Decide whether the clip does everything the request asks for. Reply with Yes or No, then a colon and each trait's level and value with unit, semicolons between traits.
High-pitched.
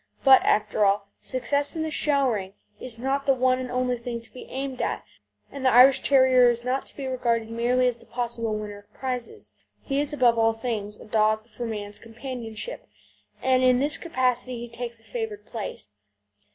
Yes: high, 245 Hz